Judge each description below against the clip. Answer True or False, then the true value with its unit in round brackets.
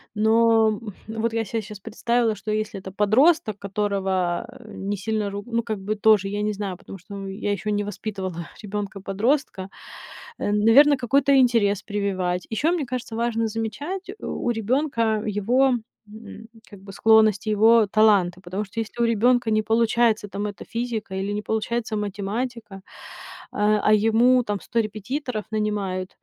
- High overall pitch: True (215 Hz)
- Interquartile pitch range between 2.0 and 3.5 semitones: True (2.5 semitones)